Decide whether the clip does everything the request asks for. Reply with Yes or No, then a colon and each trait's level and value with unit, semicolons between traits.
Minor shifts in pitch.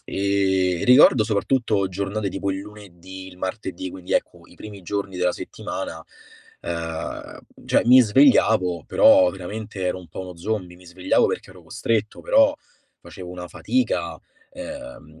No: average, 3.1 semitones